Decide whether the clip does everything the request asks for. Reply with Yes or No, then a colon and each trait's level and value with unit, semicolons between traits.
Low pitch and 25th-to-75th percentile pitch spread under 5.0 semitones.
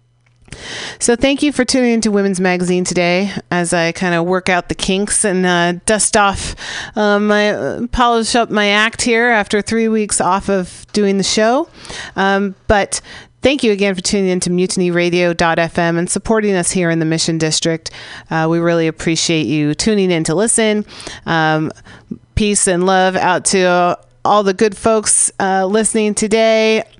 No: high, 195 Hz; average, 3.7 semitones